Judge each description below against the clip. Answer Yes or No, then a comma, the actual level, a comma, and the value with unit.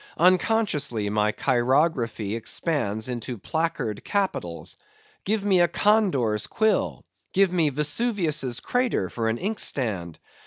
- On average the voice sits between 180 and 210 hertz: No, medium, 145 Hz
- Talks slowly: Yes, slow, 110 wpm